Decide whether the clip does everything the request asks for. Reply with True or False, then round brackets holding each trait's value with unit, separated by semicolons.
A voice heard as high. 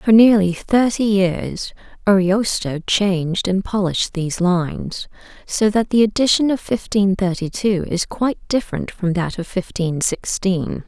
True (195 Hz)